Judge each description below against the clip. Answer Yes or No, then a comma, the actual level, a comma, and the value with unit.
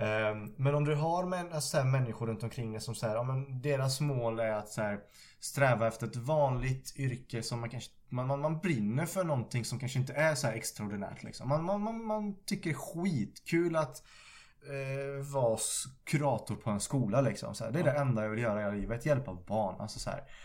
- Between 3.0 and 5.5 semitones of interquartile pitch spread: Yes, average, 4.8 semitones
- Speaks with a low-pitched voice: Yes, low, 130 Hz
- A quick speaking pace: Yes, fast, 210 wpm